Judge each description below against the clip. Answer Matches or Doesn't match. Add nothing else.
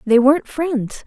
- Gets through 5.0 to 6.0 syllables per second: Doesn't match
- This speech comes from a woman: Matches